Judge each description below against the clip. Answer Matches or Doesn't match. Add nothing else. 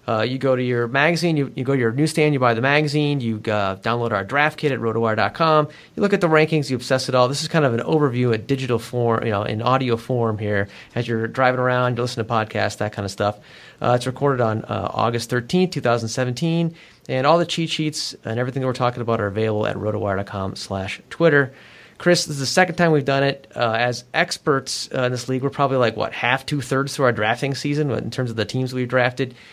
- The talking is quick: Matches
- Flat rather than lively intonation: Doesn't match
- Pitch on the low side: Matches